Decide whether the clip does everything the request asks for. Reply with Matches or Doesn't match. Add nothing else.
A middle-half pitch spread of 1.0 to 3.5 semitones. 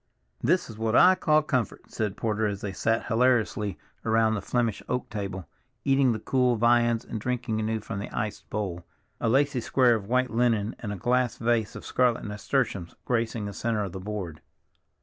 Matches